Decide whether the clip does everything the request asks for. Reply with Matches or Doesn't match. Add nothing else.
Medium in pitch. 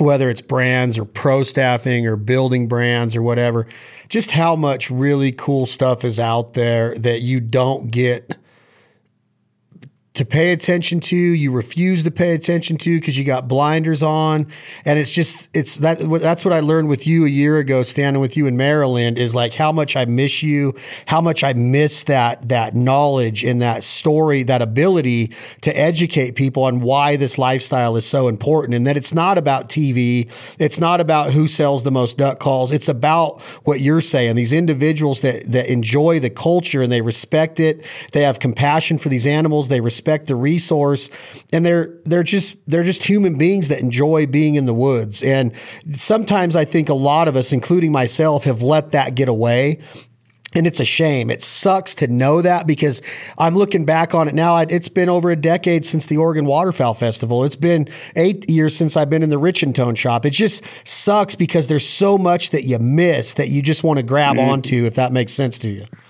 Matches